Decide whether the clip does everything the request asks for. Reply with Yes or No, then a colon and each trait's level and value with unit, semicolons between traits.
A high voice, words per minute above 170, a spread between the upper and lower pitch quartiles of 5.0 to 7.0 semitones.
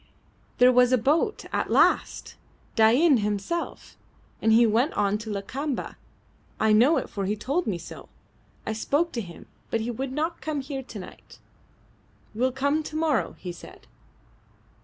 No: very high, 250 Hz; average, 160 wpm; average, 5.3 semitones